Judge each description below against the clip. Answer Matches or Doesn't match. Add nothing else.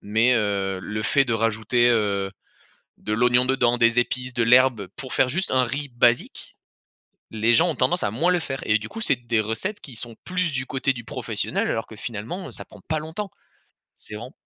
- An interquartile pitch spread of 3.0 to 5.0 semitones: Matches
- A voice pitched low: Matches